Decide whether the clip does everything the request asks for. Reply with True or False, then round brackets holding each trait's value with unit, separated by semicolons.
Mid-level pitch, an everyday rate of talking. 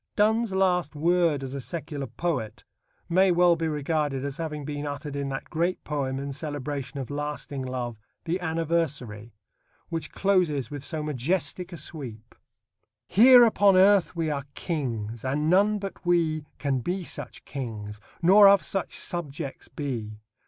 True (150 Hz; 150 wpm)